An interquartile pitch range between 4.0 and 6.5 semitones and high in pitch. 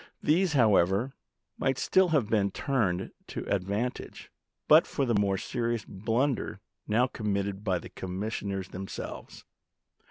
No: average, 4.4 semitones; low, 105 Hz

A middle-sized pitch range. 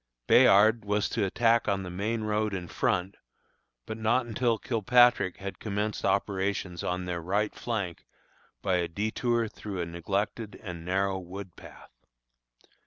Yes: average, 3.0 semitones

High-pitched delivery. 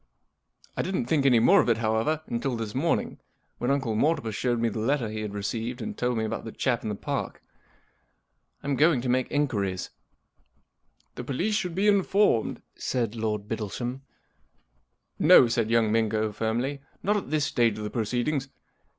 No: low, 120 Hz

